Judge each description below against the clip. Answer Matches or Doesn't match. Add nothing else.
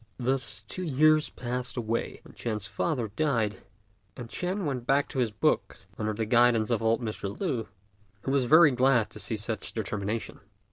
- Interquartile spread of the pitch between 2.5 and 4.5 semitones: Matches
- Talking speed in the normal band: Matches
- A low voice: Matches